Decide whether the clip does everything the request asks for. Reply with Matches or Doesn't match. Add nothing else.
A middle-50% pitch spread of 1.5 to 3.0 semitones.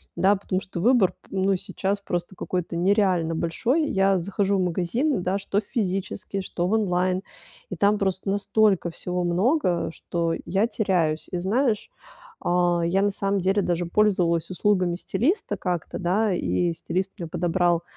Matches